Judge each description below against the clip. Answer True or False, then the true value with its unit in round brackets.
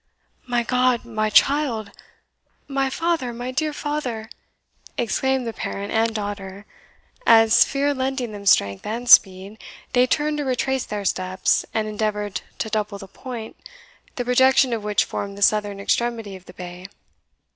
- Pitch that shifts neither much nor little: True (4.0 semitones)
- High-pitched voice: True (225 Hz)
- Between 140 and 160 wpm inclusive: True (150 wpm)